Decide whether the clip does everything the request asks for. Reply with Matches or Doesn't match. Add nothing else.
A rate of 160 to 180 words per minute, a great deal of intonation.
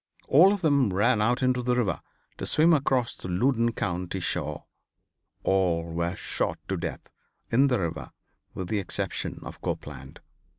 Matches